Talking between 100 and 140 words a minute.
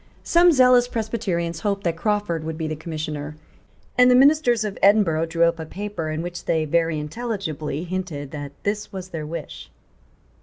No: average, 175 wpm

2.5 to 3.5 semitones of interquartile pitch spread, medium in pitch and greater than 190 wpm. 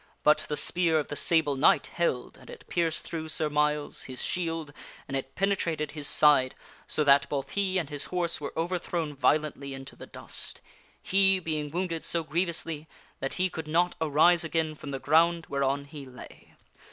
No: average, 2.9 semitones; medium, 155 Hz; average, 180 wpm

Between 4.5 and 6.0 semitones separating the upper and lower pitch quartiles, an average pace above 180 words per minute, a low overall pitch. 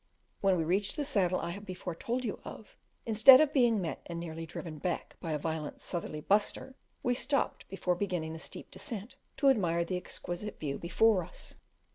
No: average, 5.0 semitones; average, 190 wpm; medium, 185 Hz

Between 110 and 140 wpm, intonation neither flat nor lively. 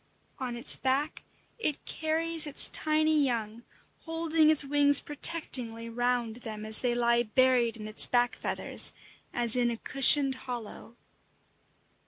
Yes: slow, 135 wpm; average, 3.9 semitones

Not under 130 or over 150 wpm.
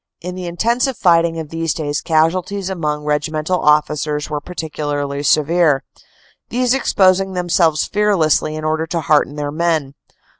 Yes: average, 140 wpm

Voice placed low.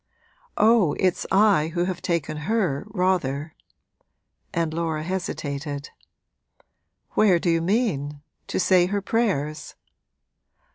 No: medium, 175 Hz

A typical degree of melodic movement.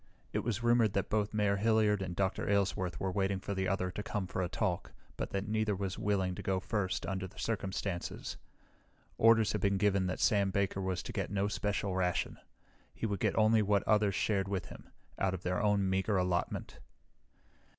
No: narrow, 1.8 semitones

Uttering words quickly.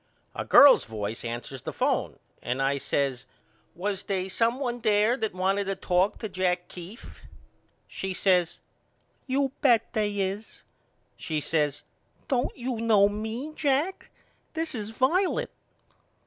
No: slow, 135 wpm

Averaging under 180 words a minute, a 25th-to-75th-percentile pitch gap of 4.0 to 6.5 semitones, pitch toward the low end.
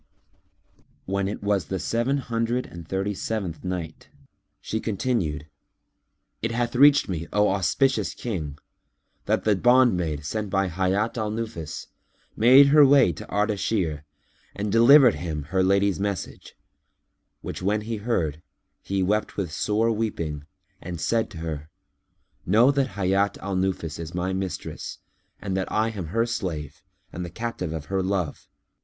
Yes: average, 150 wpm; average, 4.7 semitones; low, 100 Hz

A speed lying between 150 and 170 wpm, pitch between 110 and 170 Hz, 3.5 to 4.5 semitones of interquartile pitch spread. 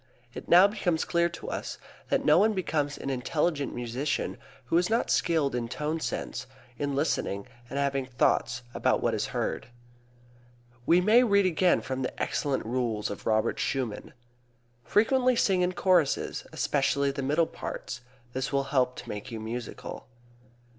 No: average, 160 wpm; medium, 140 Hz; wide, 5.6 semitones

